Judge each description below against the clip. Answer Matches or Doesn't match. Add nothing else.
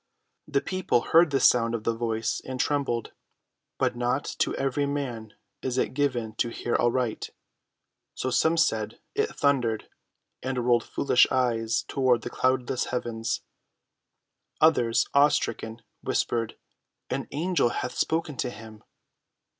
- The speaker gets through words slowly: Matches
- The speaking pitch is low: Matches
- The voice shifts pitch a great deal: Doesn't match